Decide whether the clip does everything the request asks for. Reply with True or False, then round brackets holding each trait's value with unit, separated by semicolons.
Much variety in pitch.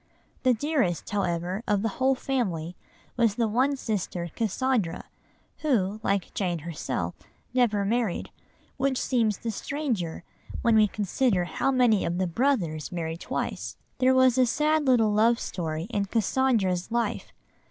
True (5.9 semitones)